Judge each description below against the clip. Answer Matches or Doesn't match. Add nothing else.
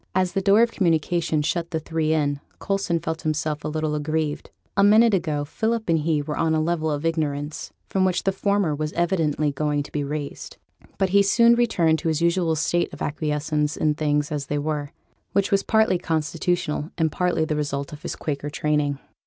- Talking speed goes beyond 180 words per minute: Matches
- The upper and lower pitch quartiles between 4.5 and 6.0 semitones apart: Doesn't match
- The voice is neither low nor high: Matches